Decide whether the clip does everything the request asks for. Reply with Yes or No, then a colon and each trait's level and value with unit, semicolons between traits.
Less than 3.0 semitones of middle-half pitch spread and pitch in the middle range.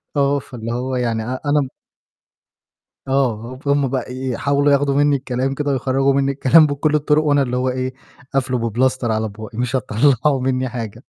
No: narrow, 2.4 semitones; low, 130 Hz